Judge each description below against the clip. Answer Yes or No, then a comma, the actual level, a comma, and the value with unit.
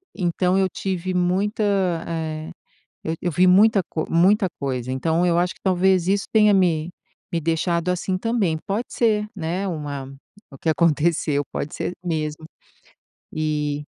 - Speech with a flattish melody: No, average, 3.3 semitones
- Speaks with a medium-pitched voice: Yes, medium, 170 Hz